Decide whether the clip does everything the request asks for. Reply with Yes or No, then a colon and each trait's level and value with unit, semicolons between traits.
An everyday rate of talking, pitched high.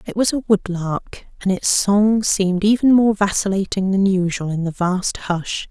Yes: average, 180 wpm; high, 195 Hz